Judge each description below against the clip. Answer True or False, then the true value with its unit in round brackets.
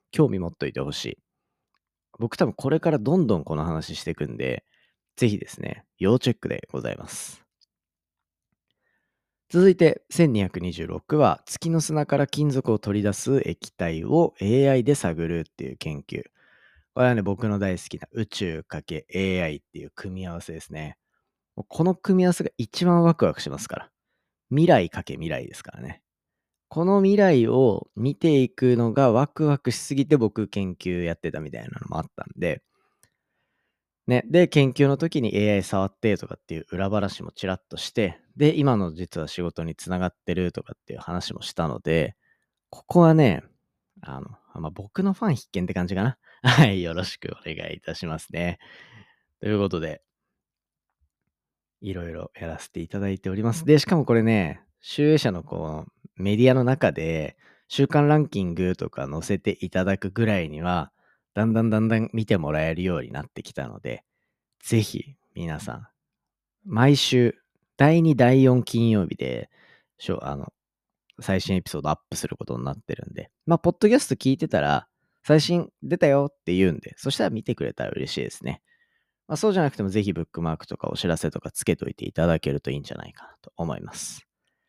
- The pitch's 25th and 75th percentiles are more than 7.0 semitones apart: True (8.0 semitones)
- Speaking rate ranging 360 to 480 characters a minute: False (335 characters per minute)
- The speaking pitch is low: True (110 Hz)